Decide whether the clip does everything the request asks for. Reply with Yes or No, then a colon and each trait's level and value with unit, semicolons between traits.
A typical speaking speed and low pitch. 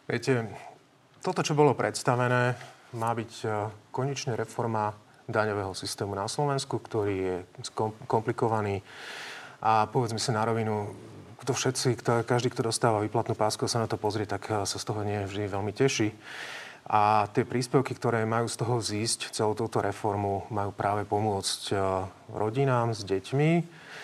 Yes: average, 140 wpm; low, 110 Hz